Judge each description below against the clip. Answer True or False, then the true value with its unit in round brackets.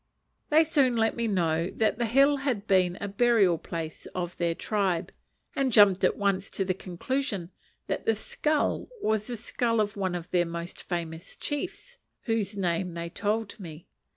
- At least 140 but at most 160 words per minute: False (175 wpm)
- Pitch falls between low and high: False (200 Hz)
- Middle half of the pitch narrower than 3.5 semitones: False (5.1 semitones)